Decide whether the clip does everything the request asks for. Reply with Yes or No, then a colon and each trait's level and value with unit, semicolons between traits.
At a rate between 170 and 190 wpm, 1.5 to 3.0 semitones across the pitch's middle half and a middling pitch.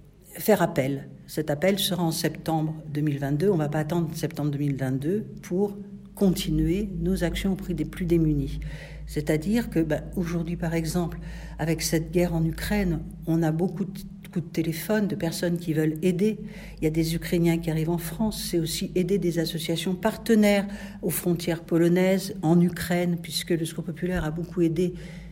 Yes: average, 175 wpm; narrow, 2.4 semitones; medium, 170 Hz